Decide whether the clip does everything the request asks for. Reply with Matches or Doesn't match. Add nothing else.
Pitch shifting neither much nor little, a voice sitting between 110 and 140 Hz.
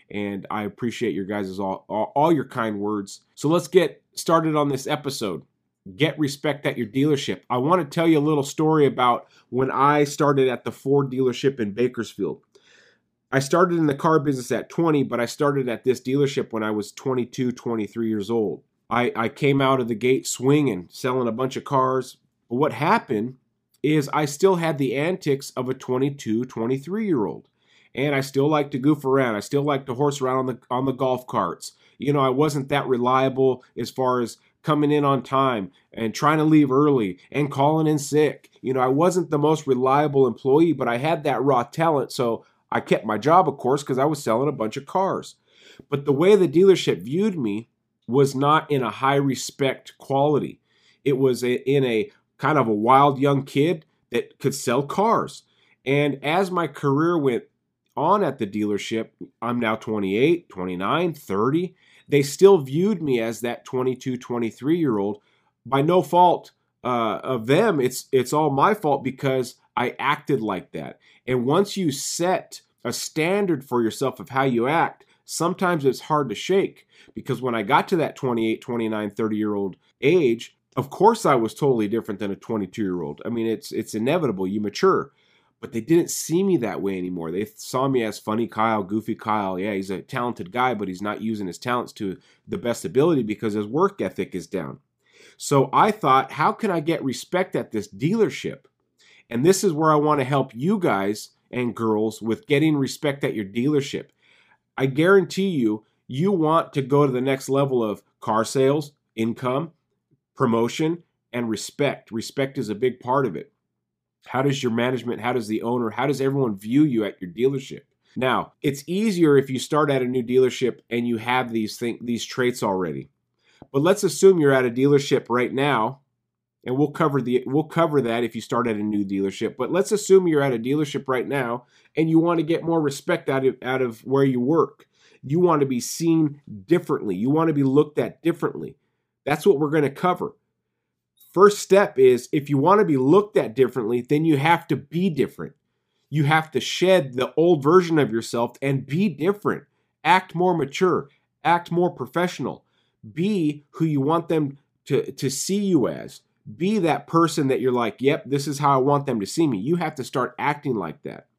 Matches